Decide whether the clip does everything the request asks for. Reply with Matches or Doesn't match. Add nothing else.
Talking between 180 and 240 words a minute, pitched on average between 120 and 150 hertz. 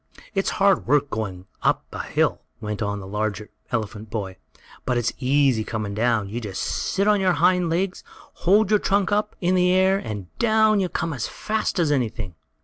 Matches